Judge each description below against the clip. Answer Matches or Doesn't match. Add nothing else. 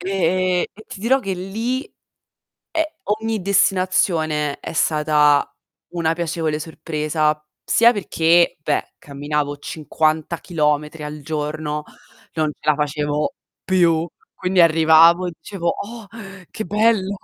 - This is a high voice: Doesn't match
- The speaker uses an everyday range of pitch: Matches